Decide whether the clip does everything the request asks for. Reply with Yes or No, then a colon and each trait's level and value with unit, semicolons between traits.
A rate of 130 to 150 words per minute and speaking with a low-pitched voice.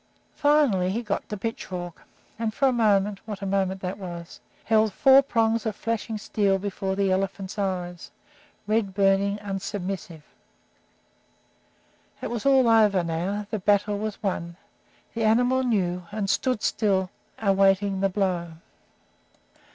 No: slow, 135 wpm; high, 200 Hz